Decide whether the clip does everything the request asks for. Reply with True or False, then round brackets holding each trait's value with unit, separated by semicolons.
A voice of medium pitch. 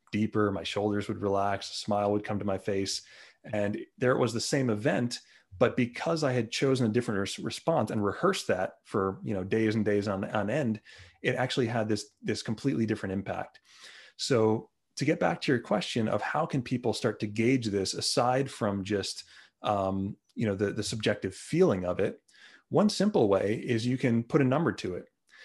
False (110 Hz)